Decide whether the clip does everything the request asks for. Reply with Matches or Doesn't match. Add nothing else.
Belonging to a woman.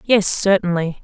Matches